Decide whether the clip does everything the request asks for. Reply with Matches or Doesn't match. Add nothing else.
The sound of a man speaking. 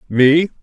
Matches